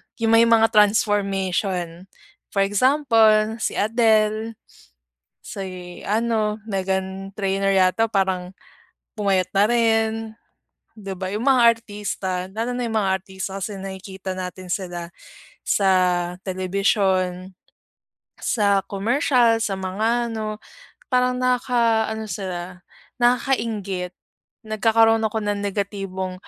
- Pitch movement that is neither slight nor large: Yes, average, 3.0 semitones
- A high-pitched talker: Yes, high, 205 Hz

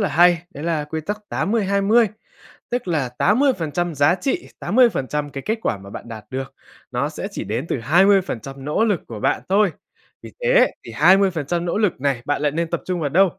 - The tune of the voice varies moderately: No, wide, 5.9 semitones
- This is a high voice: No, medium, 170 Hz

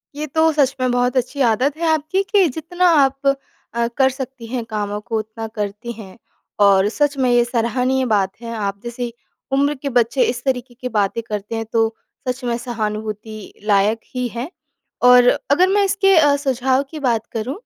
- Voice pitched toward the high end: Yes, high, 245 Hz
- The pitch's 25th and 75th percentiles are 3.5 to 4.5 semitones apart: Yes, average, 3.8 semitones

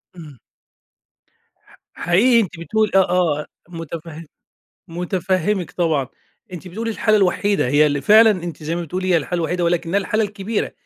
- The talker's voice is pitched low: No, medium, 180 Hz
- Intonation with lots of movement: No, average, 3.7 semitones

